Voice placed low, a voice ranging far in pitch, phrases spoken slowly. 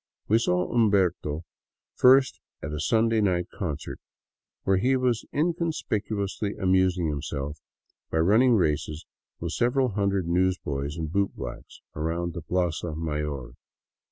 Yes: very low, 90 Hz; wide, 5.7 semitones; slow, 125 wpm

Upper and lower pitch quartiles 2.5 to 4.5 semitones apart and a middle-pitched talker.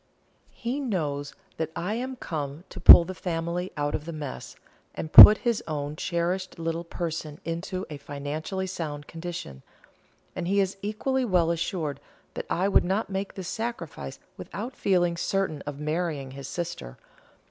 Yes: average, 4.1 semitones; medium, 170 Hz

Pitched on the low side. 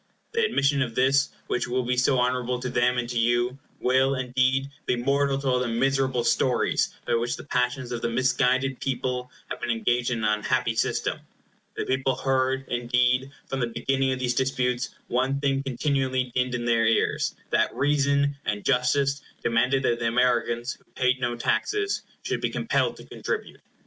Yes: low, 125 Hz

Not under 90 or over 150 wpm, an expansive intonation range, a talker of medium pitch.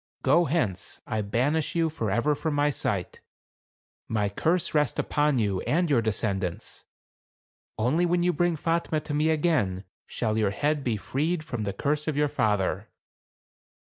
No: average, 160 wpm; wide, 6.6 semitones; medium, 145 Hz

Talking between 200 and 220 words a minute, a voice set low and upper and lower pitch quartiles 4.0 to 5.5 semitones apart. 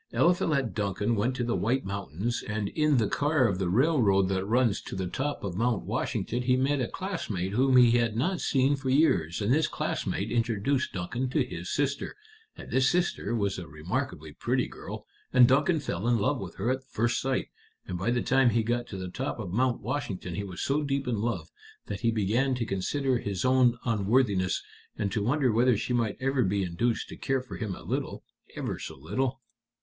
Yes: fast, 205 wpm; low, 120 Hz; average, 4.9 semitones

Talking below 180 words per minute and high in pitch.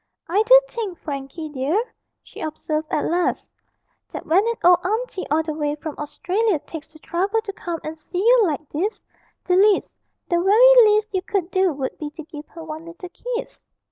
No: average, 195 wpm; very high, 350 Hz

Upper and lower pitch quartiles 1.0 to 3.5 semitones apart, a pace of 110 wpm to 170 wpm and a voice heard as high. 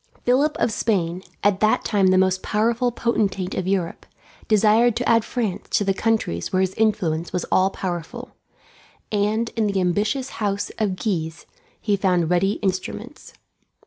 Yes: average, 3.2 semitones; average, 155 wpm; high, 200 Hz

